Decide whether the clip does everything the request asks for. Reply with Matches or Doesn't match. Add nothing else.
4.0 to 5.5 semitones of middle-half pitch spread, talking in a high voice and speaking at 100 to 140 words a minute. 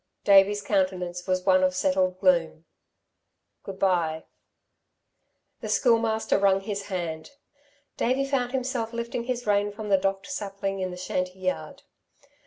Doesn't match